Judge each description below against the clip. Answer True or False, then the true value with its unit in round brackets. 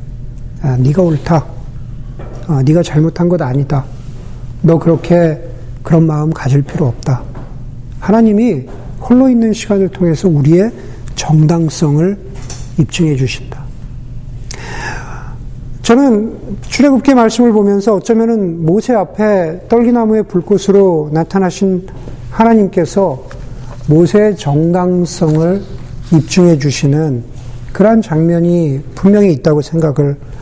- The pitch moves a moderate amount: False (6.7 semitones)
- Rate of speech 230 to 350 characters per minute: True (240 characters per minute)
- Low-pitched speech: False (155 Hz)